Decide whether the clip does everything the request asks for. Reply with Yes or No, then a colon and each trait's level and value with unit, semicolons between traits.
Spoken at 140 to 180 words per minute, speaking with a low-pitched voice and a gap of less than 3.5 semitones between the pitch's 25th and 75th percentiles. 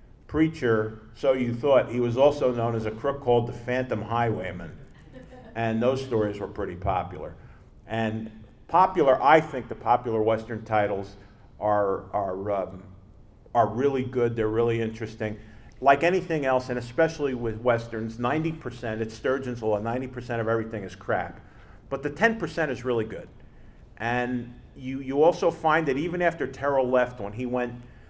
Yes: average, 160 wpm; low, 120 Hz; average, 3.0 semitones